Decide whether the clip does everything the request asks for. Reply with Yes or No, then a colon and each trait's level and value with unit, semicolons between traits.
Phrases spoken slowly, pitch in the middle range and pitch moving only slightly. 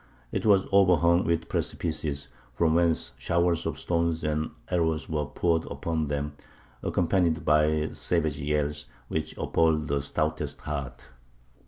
No: slow, 130 wpm; very low, 80 Hz; narrow, 2.0 semitones